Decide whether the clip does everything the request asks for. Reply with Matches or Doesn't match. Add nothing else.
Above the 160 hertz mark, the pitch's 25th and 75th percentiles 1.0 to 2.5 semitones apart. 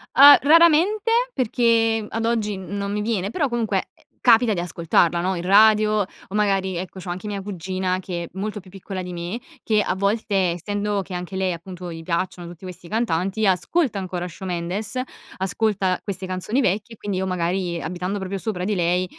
Doesn't match